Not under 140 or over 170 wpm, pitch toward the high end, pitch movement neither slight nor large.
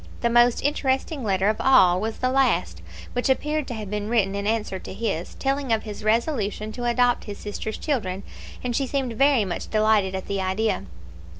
No: average, 195 wpm; high, 220 Hz; average, 3.9 semitones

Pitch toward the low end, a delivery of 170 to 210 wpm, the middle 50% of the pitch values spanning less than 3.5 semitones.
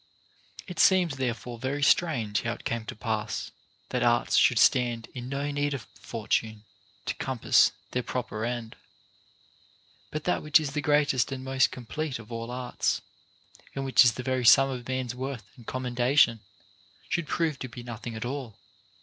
Yes: low, 125 Hz; average, 175 wpm; average, 2.9 semitones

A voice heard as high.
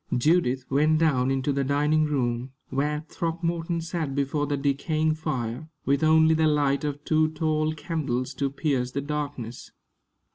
No: medium, 150 Hz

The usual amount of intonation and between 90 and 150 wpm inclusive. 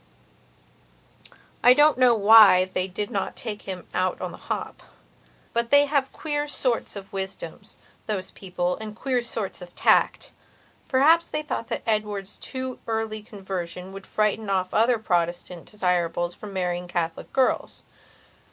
Yes: average, 4.6 semitones; average, 145 wpm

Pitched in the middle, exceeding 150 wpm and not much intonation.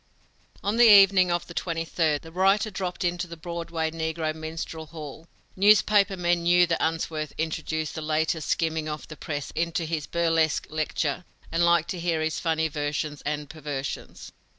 Yes: medium, 165 Hz; average, 170 wpm; narrow, 1.8 semitones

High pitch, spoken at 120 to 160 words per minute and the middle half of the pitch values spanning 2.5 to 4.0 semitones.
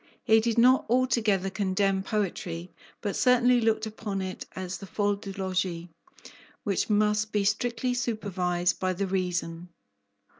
Yes: high, 200 Hz; average, 140 wpm; average, 3.0 semitones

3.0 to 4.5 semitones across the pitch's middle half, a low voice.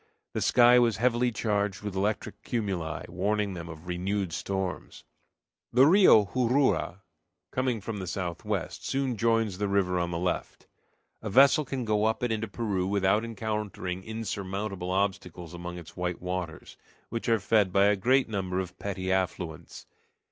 Yes: average, 3.7 semitones; low, 100 Hz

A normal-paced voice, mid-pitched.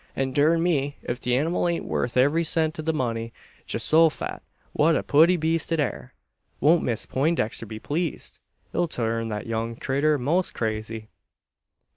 Yes: average, 160 wpm; medium, 145 Hz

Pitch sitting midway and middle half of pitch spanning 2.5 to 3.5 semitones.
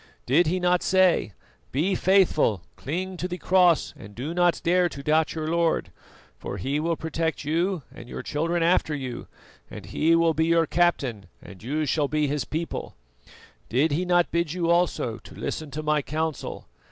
Yes: medium, 160 Hz; average, 3.1 semitones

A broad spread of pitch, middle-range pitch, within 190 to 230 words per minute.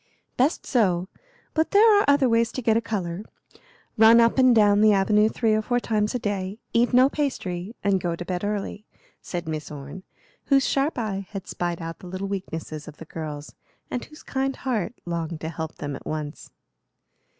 No: wide, 5.7 semitones; high, 205 Hz; average, 195 wpm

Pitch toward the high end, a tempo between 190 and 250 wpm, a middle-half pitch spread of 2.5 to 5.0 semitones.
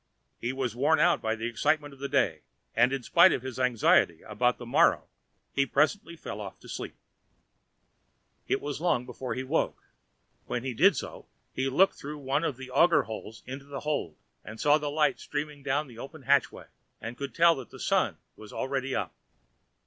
No: low, 135 Hz; average, 195 wpm; average, 3.4 semitones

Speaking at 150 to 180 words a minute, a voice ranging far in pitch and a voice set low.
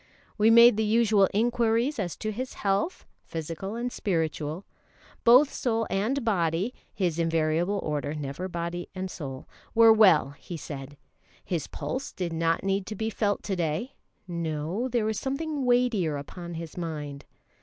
No: average, 155 wpm; wide, 5.7 semitones; high, 190 Hz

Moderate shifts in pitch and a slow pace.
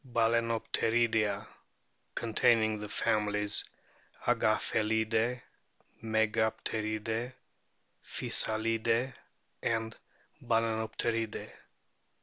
No: narrow, 0.9 semitones; slow, 50 wpm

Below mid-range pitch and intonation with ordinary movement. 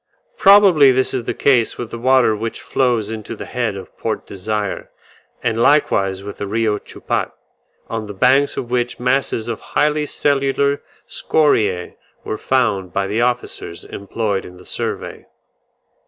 Yes: low, 115 Hz; average, 4.3 semitones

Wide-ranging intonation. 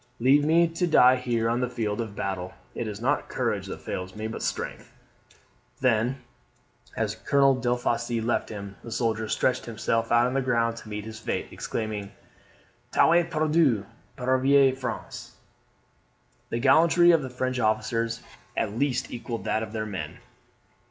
No: average, 3.3 semitones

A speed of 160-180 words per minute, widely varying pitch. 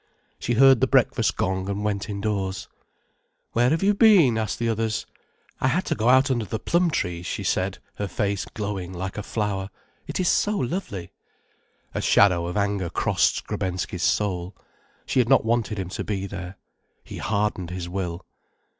No: average, 175 wpm; average, 4.2 semitones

